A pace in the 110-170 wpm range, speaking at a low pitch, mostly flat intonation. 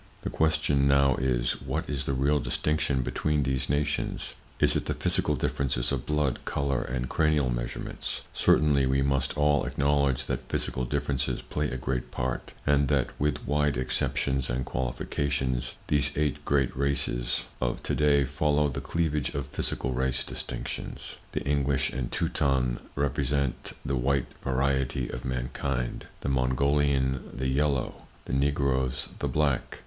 Yes: average, 150 wpm; very low, 70 Hz; narrow, 2.1 semitones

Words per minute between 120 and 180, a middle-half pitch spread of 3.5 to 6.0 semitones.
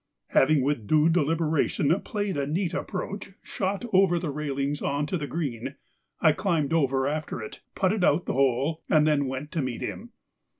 Yes: average, 175 wpm; average, 3.9 semitones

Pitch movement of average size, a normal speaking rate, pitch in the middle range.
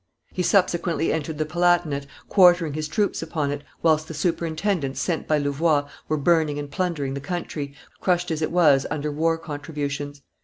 Yes: average, 3.0 semitones; average, 165 wpm; medium, 155 Hz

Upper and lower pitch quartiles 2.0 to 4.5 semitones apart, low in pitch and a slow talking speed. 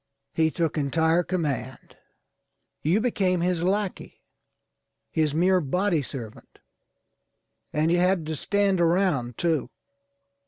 No: average, 3.2 semitones; medium, 170 Hz; slow, 110 wpm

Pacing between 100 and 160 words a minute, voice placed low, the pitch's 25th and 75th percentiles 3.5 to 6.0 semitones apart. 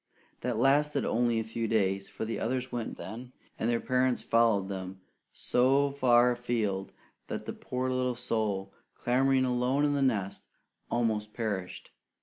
No: average, 150 wpm; low, 120 Hz; average, 2.9 semitones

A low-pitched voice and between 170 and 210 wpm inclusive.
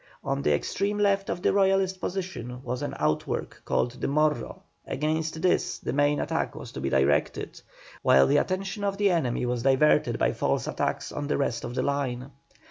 No: medium, 145 Hz; average, 190 wpm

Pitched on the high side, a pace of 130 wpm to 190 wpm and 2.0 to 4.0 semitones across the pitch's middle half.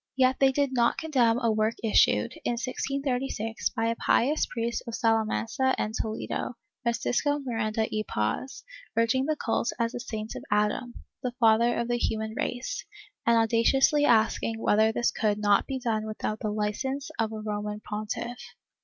Yes: high, 230 Hz; average, 170 wpm; average, 2.8 semitones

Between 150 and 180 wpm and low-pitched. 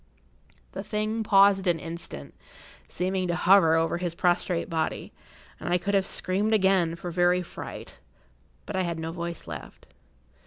No: average, 155 wpm; medium, 180 Hz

